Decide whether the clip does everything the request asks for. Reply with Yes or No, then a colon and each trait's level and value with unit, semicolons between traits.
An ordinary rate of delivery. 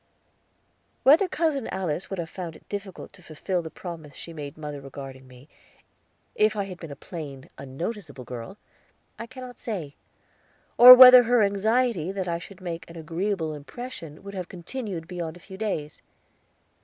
Yes: average, 165 wpm